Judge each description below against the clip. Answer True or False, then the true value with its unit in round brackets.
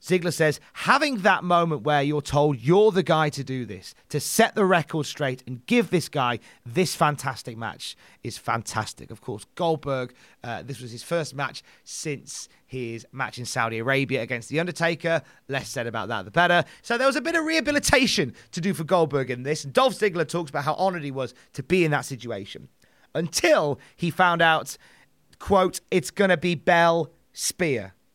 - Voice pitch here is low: False (150 Hz)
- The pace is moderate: True (190 wpm)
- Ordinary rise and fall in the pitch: False (5.8 semitones)